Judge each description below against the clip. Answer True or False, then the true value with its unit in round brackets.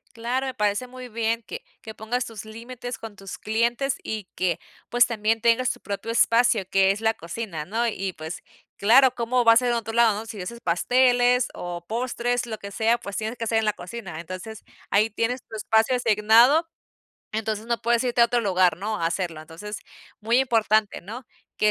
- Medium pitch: False (225 Hz)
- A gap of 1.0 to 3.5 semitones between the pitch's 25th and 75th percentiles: True (2.8 semitones)